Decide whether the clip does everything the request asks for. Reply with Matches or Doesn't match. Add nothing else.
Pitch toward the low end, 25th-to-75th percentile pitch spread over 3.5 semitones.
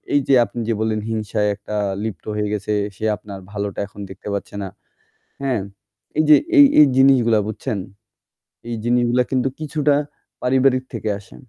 Matches